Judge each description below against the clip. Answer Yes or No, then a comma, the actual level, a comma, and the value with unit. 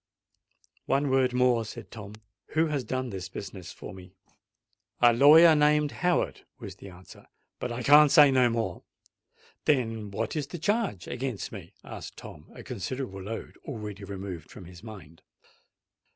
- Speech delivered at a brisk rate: No, average, 155 wpm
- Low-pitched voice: Yes, low, 120 Hz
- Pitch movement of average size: No, wide, 6.1 semitones